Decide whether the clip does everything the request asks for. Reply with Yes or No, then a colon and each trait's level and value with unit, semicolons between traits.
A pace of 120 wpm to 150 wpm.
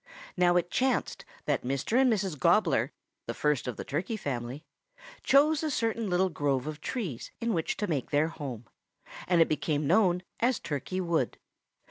No: average, 170 wpm